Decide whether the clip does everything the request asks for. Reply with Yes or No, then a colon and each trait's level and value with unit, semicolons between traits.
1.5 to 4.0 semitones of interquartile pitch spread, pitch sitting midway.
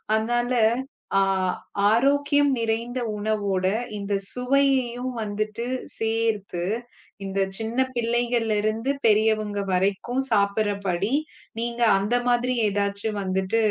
No: average, 3.1 semitones; high, 220 Hz